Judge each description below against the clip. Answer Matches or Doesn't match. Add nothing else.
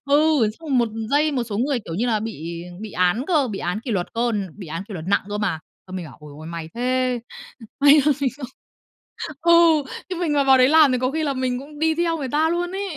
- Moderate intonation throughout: Doesn't match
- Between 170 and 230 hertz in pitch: Doesn't match